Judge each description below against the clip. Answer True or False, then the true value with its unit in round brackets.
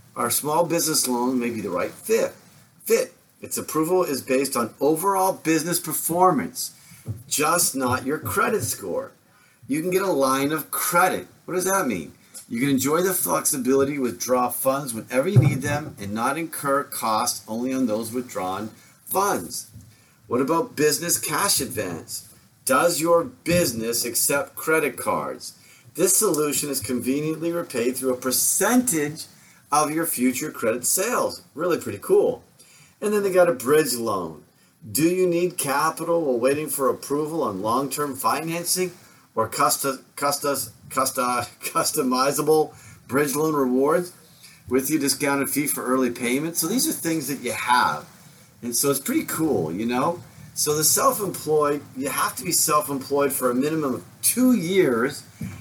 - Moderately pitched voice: True (145 Hz)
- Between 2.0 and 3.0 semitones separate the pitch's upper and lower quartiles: False (4.7 semitones)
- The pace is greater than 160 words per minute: False (155 wpm)